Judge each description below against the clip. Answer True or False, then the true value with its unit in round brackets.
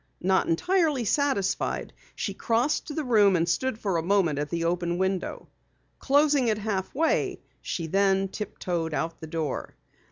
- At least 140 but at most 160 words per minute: True (155 wpm)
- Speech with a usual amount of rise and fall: False (6.8 semitones)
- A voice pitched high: True (195 Hz)